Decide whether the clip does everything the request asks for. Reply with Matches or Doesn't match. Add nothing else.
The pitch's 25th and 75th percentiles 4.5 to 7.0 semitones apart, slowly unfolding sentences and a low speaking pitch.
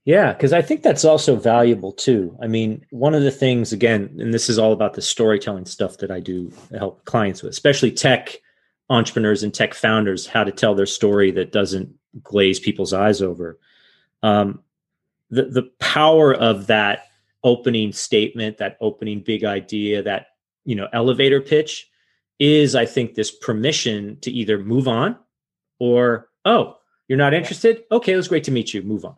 Doesn't match